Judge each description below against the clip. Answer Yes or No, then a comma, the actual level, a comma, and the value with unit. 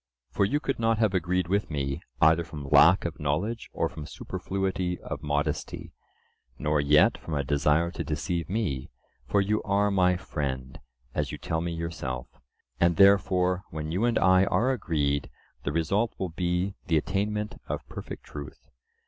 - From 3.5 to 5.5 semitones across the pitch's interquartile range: Yes, average, 4.6 semitones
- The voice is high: No, very low, 85 Hz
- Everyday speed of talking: Yes, average, 165 wpm